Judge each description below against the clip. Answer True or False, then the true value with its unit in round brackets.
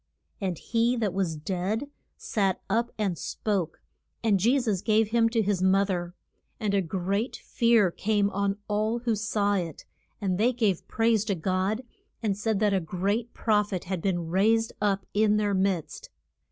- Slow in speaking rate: False (175 wpm)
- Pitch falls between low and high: False (205 Hz)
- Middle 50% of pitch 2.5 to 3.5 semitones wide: True (2.8 semitones)